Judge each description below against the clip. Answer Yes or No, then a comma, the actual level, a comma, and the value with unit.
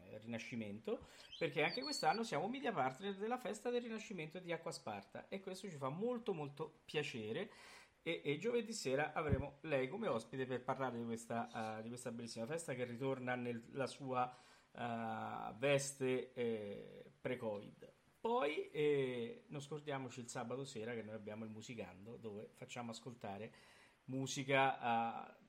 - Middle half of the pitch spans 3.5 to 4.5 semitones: No, average, 5.0 semitones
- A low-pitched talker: Yes, low, 130 Hz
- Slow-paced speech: No, average, 150 wpm